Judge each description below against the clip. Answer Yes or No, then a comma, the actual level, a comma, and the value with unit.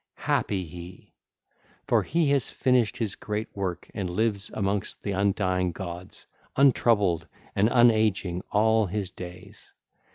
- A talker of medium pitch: No, low, 100 Hz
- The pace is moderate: No, slow, 125 wpm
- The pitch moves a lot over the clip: No, average, 3.3 semitones